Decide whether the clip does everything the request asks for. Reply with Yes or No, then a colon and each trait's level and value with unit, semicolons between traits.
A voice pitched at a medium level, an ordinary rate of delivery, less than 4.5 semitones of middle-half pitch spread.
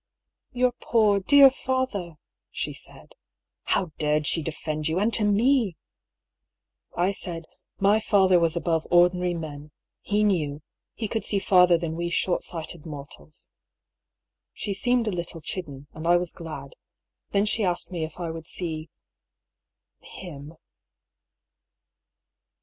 Yes: medium, 175 Hz; average, 155 wpm; average, 4.0 semitones